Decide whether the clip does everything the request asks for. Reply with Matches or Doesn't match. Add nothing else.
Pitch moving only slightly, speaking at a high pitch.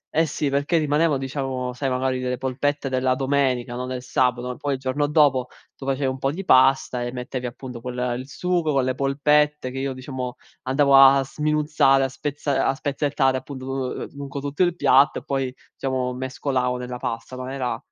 Doesn't match